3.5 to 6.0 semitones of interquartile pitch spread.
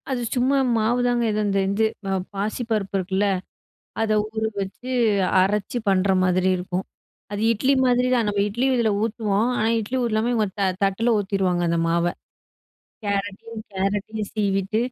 No: average, 2.8 semitones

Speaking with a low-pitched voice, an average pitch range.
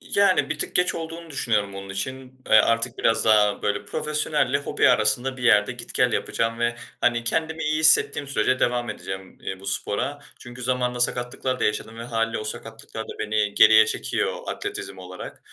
Yes: low, 120 Hz; average, 3.7 semitones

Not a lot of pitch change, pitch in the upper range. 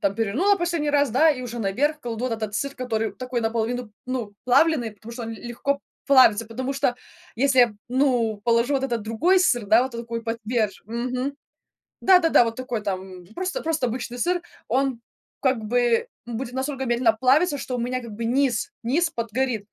No: average, 3.1 semitones; high, 245 Hz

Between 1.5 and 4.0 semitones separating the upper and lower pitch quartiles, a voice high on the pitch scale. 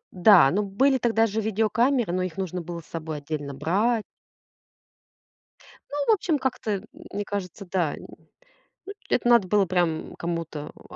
No: average, 4.8 semitones; high, 195 Hz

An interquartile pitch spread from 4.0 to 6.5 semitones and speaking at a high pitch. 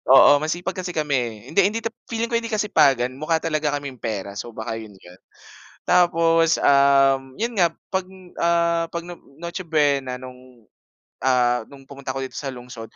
No: average, 4.8 semitones; medium, 140 Hz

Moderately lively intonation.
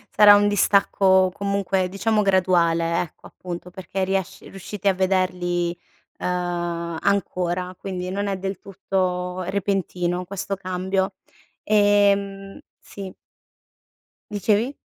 No: narrow, 1.7 semitones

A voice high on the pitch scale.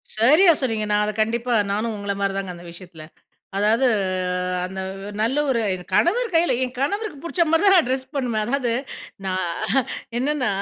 Yes: high, 240 Hz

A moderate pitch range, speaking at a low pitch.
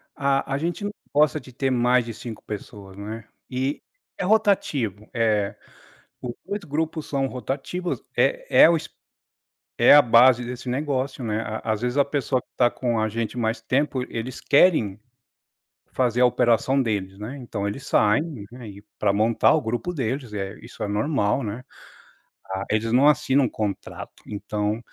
Yes: average, 4.3 semitones; low, 125 Hz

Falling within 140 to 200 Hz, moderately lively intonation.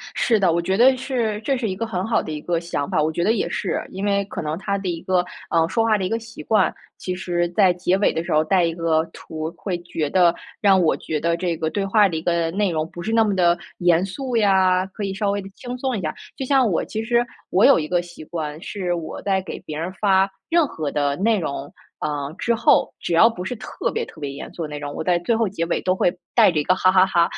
Yes: medium, 185 Hz; average, 3.8 semitones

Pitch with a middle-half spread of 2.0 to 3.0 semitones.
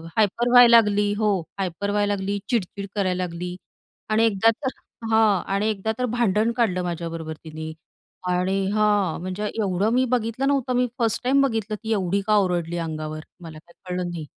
No: average, 3.9 semitones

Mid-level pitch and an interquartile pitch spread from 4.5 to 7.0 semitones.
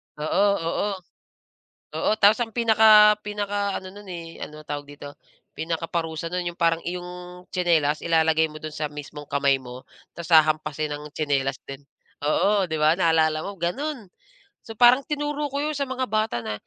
Yes: medium, 170 Hz; average, 5.2 semitones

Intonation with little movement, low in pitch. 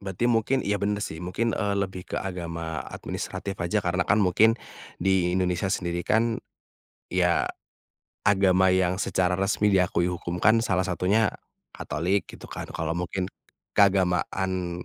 Yes: narrow, 2.3 semitones; very low, 95 Hz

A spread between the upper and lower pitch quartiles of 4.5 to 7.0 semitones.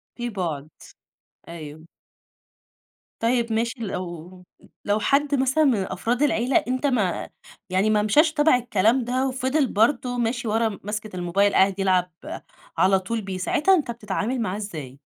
Yes: average, 5.1 semitones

